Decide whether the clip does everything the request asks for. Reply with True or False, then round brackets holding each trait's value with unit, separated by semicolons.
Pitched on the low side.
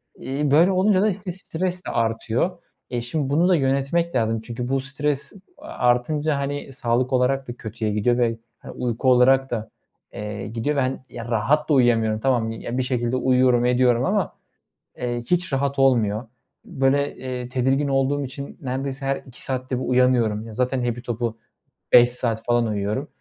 True (130 Hz)